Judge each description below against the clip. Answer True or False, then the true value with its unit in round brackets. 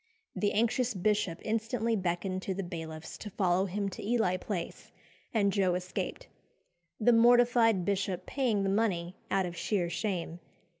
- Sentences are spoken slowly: False (150 wpm)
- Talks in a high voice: True (195 Hz)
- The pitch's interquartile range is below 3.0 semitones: False (3.7 semitones)